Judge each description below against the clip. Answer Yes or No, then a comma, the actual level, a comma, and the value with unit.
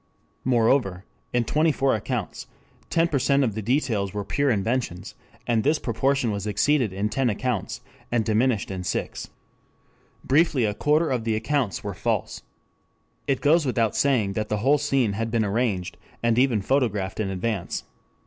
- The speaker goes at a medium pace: Yes, average, 160 wpm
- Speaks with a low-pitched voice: Yes, low, 115 Hz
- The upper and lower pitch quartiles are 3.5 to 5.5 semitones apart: Yes, average, 4.6 semitones